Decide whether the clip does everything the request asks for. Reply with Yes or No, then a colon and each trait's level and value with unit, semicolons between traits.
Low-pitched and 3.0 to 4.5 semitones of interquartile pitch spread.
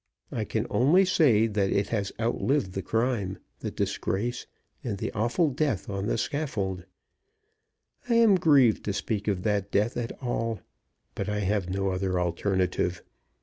Yes: low, 105 Hz; average, 4.0 semitones